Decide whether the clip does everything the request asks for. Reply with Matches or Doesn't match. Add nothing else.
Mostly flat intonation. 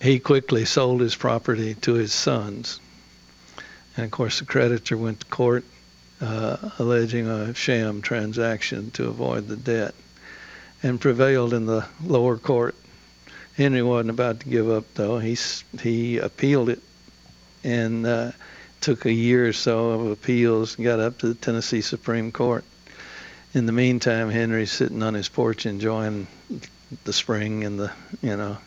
Matches